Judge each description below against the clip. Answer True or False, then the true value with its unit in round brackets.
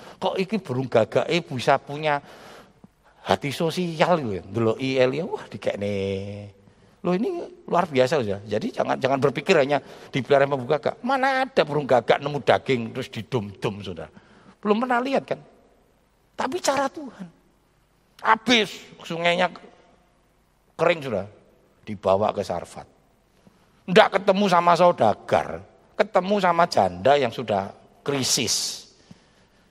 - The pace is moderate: True (115 wpm)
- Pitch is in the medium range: True (170 Hz)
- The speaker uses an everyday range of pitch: False (8.3 semitones)